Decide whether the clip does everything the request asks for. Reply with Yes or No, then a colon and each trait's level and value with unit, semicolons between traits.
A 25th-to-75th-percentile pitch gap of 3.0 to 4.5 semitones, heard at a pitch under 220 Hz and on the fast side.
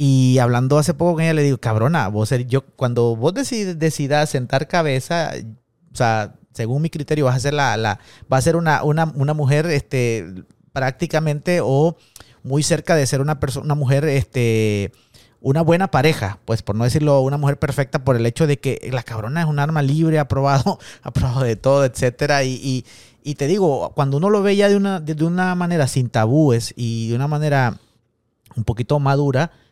Yes: average, 4.2 semitones; medium, 140 Hz; fast, 195 wpm